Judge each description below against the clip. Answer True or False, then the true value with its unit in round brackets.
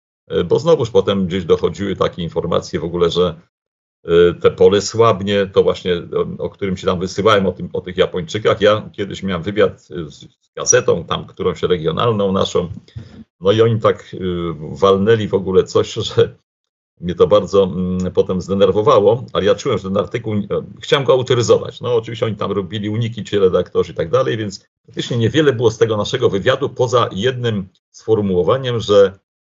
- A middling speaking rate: False (165 wpm)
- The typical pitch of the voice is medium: False (130 Hz)